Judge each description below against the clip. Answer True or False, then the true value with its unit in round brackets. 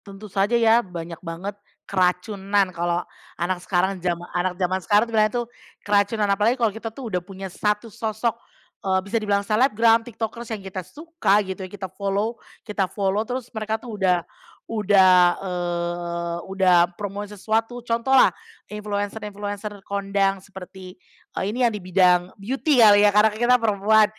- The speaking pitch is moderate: False (200 Hz)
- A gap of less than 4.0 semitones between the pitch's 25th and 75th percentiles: True (2.9 semitones)